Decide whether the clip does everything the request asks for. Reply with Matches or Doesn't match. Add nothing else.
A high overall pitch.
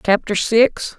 Matches